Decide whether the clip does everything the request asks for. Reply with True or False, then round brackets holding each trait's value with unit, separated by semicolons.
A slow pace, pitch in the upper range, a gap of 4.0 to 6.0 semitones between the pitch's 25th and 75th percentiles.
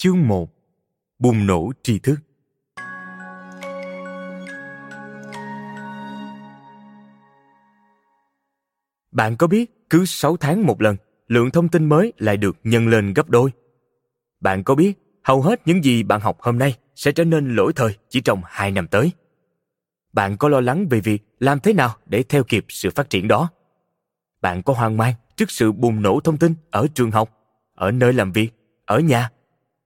False (160 wpm; 115 Hz; 5.6 semitones)